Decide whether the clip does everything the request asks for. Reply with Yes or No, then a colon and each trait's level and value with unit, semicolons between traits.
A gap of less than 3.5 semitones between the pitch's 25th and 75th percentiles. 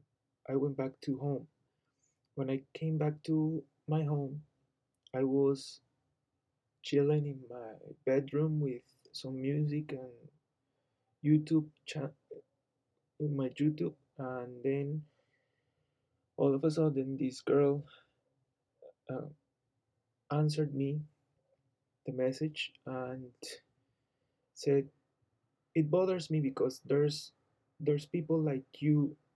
Yes: narrow, 2.4 semitones